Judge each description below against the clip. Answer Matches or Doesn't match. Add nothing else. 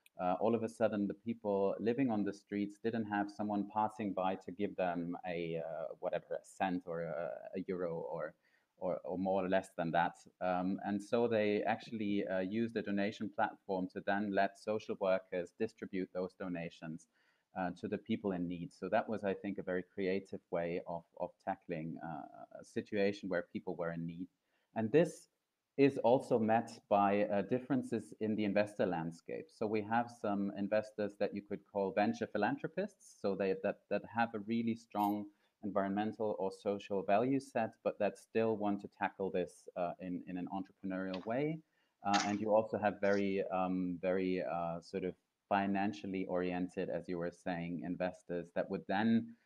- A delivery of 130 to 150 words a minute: Doesn't match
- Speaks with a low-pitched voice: Matches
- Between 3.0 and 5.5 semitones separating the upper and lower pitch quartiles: Doesn't match